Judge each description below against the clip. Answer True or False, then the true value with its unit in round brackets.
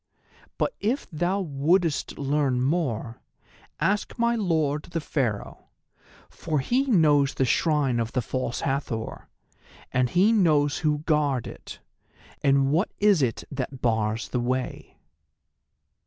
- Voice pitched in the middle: True (145 Hz)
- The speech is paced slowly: True (125 wpm)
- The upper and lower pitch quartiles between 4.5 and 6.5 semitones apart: True (5.1 semitones)